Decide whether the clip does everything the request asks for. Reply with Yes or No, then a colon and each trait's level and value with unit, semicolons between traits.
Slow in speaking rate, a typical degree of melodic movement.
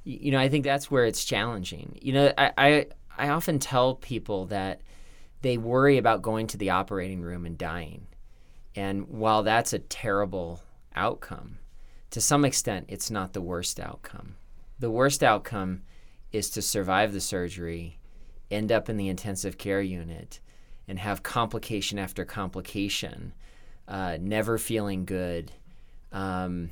No: average, 150 wpm; average, 4.1 semitones